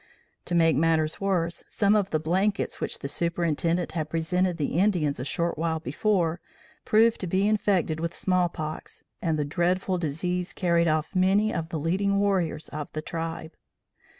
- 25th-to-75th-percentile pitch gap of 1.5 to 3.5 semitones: Yes, average, 2.8 semitones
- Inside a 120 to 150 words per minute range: No, average, 170 wpm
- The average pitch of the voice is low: No, medium, 170 Hz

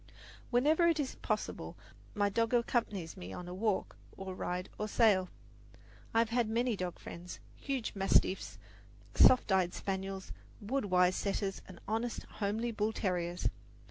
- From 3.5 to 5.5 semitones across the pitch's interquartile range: Yes, average, 3.9 semitones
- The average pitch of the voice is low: No, high, 205 Hz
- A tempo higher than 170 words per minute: No, average, 145 wpm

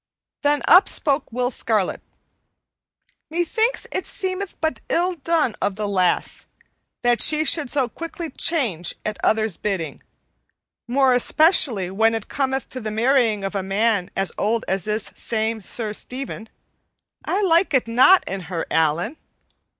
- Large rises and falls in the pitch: Yes, wide, 6.9 semitones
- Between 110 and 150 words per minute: Yes, average, 145 wpm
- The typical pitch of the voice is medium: No, high, 235 Hz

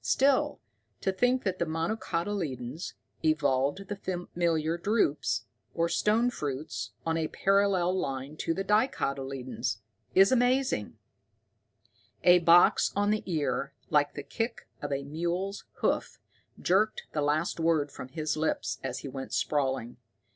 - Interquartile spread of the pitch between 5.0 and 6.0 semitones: Yes, wide, 5.6 semitones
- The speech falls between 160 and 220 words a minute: No, slow, 135 wpm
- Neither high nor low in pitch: Yes, medium, 165 Hz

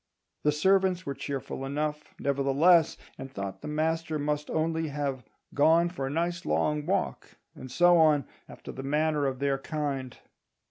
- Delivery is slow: No, average, 155 wpm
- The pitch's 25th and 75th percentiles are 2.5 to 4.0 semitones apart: Yes, average, 2.9 semitones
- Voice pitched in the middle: Yes, medium, 150 Hz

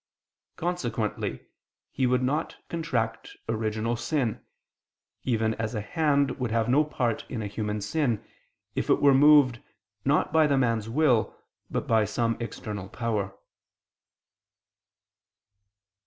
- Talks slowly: Yes, slow, 125 wpm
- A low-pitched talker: Yes, low, 115 Hz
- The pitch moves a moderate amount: Yes, average, 4.2 semitones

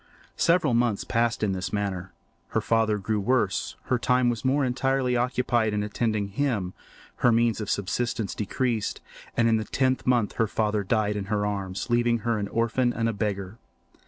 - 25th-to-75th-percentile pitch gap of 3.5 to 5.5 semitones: No, average, 2.9 semitones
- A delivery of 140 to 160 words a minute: No, average, 180 wpm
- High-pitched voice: No, low, 115 Hz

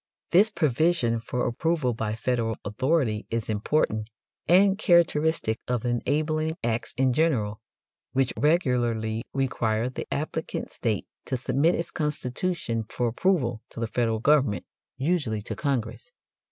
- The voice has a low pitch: Yes, low, 125 Hz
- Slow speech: Yes, slow, 125 wpm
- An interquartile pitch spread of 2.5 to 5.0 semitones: No, wide, 5.6 semitones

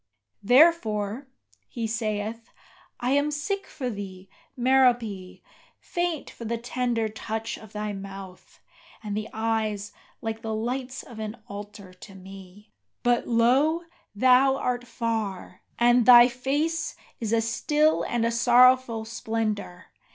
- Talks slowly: Yes, slow, 130 wpm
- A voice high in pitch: Yes, high, 230 Hz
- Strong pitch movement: No, average, 3.1 semitones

